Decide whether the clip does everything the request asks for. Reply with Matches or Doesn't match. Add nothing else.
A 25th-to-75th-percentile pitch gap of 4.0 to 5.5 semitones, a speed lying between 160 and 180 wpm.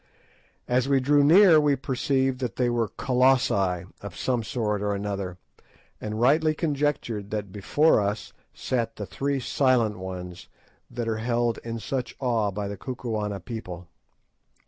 Doesn't match